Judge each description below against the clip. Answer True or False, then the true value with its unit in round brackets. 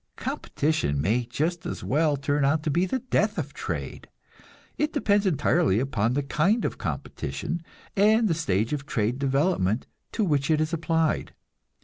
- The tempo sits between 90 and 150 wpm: False (160 wpm)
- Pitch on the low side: False (155 Hz)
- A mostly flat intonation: False (4.5 semitones)